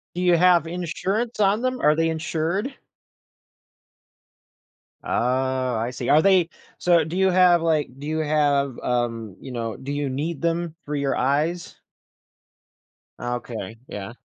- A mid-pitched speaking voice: Yes, medium, 155 Hz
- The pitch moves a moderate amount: Yes, average, 5.0 semitones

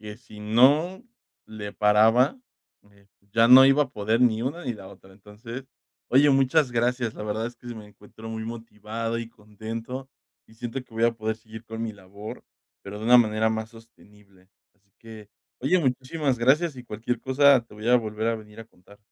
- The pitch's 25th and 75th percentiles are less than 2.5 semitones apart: No, average, 2.8 semitones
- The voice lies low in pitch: Yes, low, 115 Hz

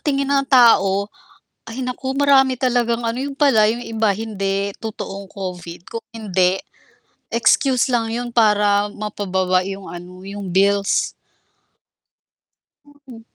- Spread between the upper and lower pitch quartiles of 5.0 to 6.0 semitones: No, average, 3.8 semitones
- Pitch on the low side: No, high, 215 Hz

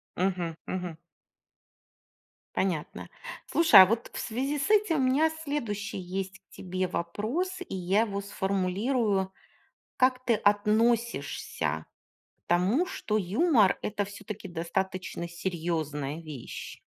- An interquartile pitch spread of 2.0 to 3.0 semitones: No, average, 4.8 semitones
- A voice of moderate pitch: No, high, 195 Hz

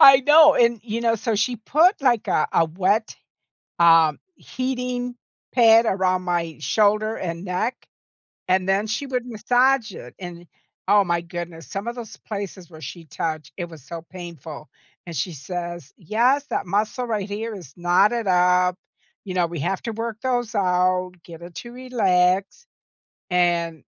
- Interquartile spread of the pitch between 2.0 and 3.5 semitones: No, average, 5.2 semitones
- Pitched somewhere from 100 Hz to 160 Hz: No, high, 190 Hz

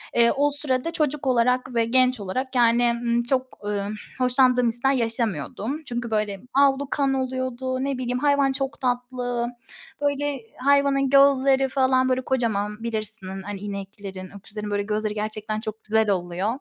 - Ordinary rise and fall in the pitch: Yes, average, 3.7 semitones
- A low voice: No, high, 245 Hz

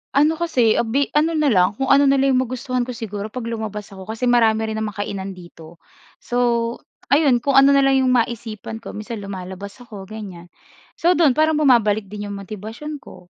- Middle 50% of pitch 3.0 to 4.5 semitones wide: No, average, 4.9 semitones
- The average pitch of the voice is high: Yes, high, 230 Hz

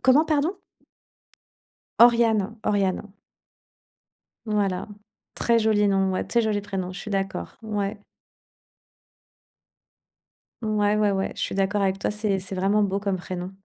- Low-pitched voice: No, high, 205 Hz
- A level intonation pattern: Yes, narrow, 2.0 semitones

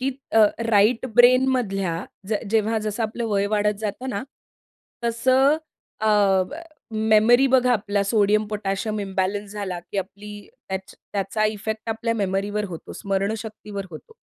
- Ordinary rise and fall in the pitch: No, narrow, 2.3 semitones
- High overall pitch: Yes, high, 210 Hz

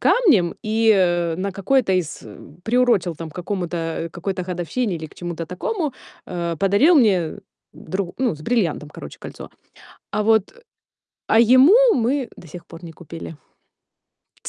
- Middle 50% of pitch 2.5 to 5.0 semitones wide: No, wide, 5.4 semitones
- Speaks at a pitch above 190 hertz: No, medium, 185 Hz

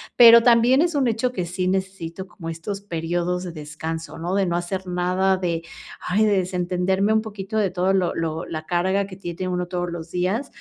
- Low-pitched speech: No, medium, 185 Hz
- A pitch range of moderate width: No, narrow, 2.3 semitones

